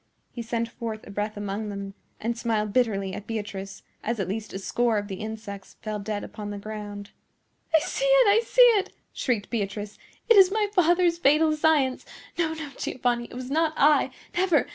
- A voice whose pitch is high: Yes, high, 230 Hz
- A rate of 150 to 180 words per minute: No, average, 190 wpm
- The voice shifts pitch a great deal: Yes, wide, 7.2 semitones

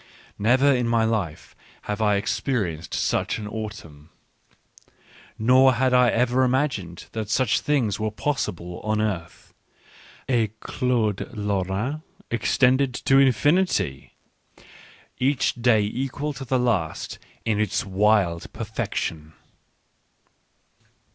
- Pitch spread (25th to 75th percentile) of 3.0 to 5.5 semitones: Yes, average, 4.1 semitones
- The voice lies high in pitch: No, low, 110 Hz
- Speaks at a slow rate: Yes, slow, 110 wpm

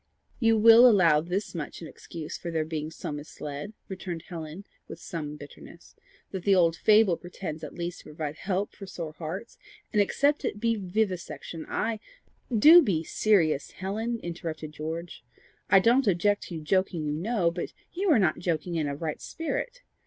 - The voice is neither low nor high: Yes, medium, 175 Hz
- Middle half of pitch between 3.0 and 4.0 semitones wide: No, average, 4.9 semitones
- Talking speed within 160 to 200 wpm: Yes, average, 175 wpm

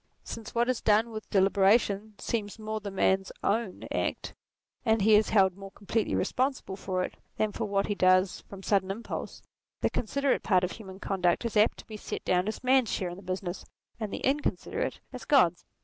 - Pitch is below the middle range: No, high, 205 Hz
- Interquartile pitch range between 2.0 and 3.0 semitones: Yes, narrow, 2.6 semitones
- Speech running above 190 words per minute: Yes, average, 200 wpm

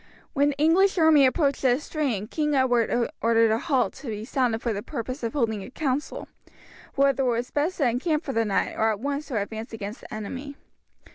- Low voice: No, very high, 255 Hz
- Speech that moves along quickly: Yes, fast, 210 wpm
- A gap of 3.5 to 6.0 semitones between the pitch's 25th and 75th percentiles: Yes, average, 4.1 semitones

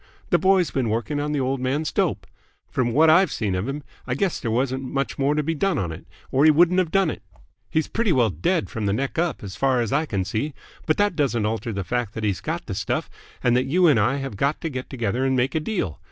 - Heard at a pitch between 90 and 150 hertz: Yes, low, 135 Hz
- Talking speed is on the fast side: Yes, fast, 265 wpm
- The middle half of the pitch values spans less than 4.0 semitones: No, wide, 5.4 semitones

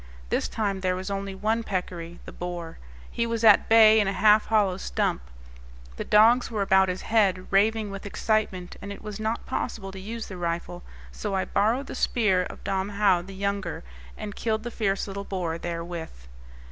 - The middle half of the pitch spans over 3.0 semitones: No, average, 2.7 semitones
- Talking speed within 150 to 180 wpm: No, average, 190 wpm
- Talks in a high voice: Yes, high, 200 Hz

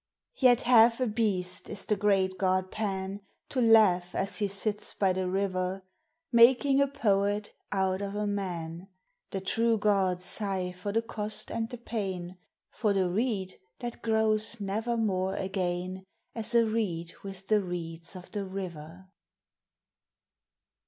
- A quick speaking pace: No, average, 145 wpm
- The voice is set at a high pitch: Yes, high, 195 Hz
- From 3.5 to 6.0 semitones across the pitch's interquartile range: No, average, 2.9 semitones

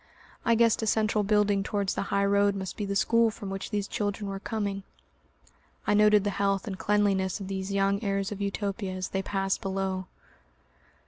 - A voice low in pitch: No, high, 200 Hz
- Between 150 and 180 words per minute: No, average, 190 wpm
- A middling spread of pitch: No, narrow, 1.2 semitones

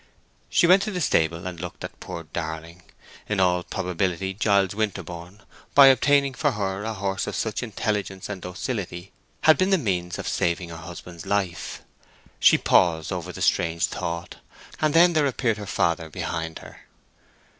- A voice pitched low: Yes, very low, 95 Hz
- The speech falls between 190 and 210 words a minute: No, average, 165 wpm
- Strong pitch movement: No, average, 4.5 semitones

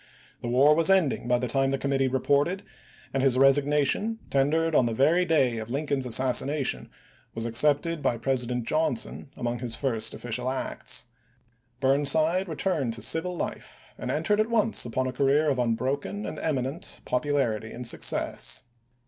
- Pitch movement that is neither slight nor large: Yes, average, 3.8 semitones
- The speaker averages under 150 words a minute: No, average, 165 wpm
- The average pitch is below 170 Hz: Yes, low, 135 Hz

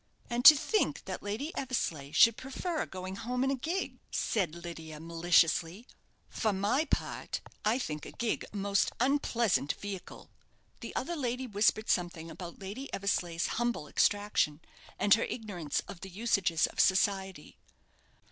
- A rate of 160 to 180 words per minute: No, average, 145 wpm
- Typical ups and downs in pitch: No, wide, 5.8 semitones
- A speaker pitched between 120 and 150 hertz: No, high, 205 Hz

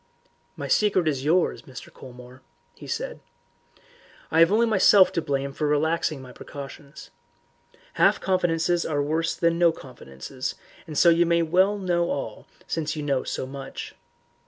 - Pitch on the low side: No, medium, 160 Hz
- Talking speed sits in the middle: Yes, average, 150 wpm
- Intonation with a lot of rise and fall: No, average, 3.8 semitones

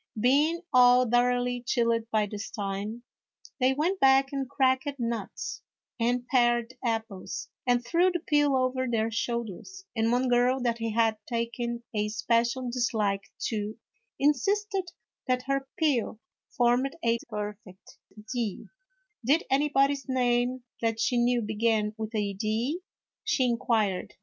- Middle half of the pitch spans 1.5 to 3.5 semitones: Yes, average, 2.9 semitones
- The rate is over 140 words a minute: No, slow, 135 wpm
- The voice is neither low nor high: No, high, 240 Hz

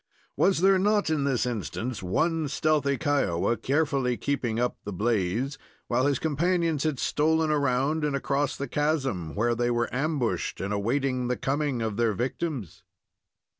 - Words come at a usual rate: Yes, average, 155 wpm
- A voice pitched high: No, low, 135 Hz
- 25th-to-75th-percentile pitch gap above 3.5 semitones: Yes, average, 4.4 semitones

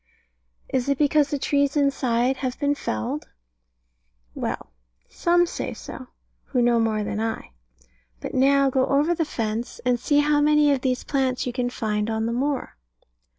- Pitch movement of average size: Yes, average, 3.4 semitones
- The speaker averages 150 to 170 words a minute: Yes, average, 165 wpm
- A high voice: Yes, very high, 260 Hz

